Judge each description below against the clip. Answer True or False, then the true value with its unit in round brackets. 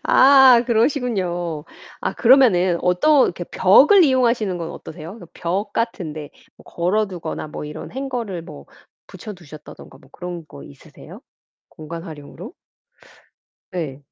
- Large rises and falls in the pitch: True (6.2 semitones)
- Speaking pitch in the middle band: True (180 Hz)